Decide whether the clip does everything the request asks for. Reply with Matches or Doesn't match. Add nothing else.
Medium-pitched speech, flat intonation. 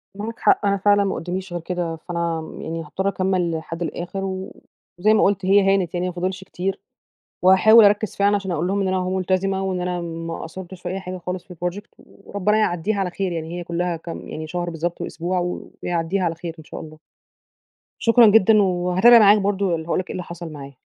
Matches